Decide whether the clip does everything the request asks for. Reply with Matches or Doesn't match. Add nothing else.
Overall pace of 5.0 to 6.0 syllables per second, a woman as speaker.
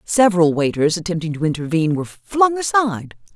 Doesn't match